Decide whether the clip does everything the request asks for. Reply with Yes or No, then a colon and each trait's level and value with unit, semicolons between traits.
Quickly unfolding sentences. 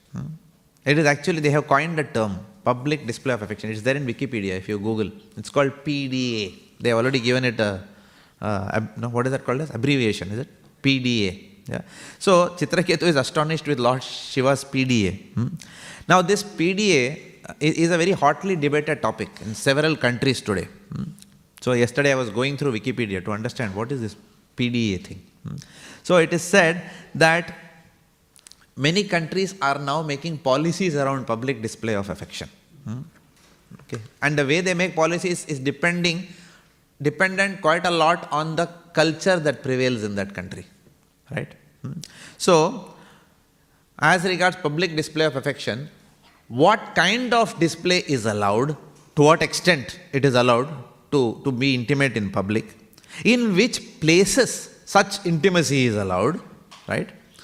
No: average, 160 wpm